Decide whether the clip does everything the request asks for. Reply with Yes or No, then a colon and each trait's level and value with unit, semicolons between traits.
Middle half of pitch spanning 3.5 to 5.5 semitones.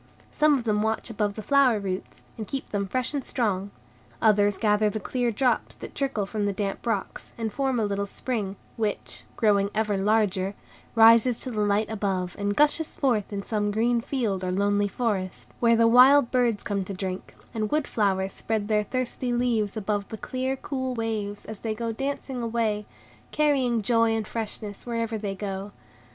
No: average, 3.0 semitones